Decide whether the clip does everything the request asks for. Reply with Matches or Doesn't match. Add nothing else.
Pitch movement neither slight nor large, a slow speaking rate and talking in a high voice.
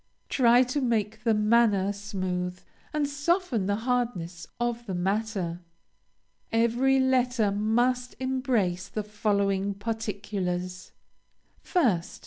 Matches